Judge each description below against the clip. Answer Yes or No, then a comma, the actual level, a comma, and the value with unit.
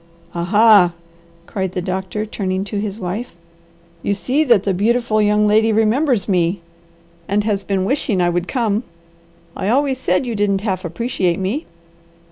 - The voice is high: Yes, high, 205 Hz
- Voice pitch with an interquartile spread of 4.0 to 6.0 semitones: No, average, 3.2 semitones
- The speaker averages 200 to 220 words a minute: No, average, 160 wpm